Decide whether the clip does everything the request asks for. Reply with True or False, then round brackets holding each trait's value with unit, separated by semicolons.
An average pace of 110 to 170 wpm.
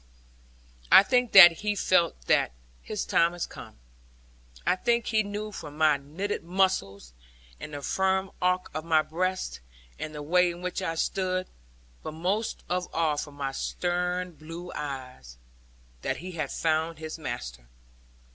True (155 wpm)